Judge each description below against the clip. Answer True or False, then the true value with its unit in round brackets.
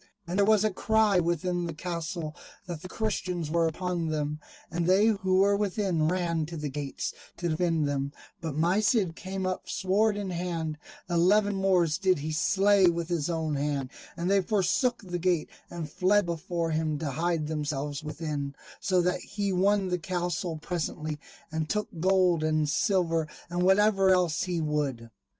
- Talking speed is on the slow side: False (175 wpm)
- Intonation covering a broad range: False (3.3 semitones)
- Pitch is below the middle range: False (175 Hz)